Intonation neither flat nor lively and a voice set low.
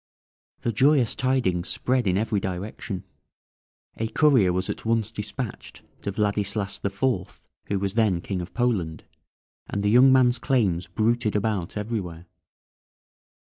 Yes: average, 3.9 semitones; low, 105 Hz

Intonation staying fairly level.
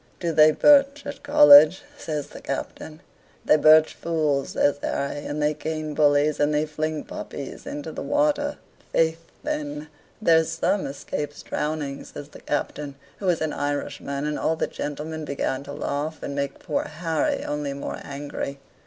Yes: narrow, 2.0 semitones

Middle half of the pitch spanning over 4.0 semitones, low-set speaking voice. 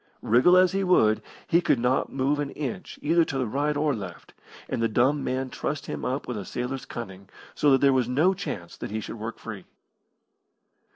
Yes: average, 4.4 semitones; low, 130 Hz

